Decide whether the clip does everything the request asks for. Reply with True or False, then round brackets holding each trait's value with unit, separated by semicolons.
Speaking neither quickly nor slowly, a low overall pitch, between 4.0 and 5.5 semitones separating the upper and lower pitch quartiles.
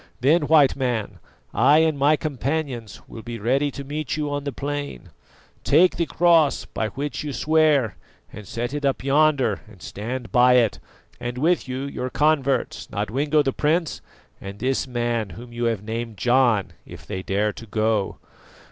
True (170 wpm; 130 Hz; 4.3 semitones)